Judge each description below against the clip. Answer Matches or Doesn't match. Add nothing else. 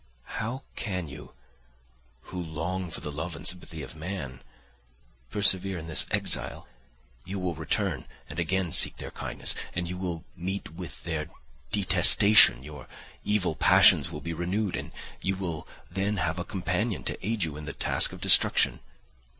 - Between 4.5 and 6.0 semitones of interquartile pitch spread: Doesn't match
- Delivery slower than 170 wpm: Matches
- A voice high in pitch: Doesn't match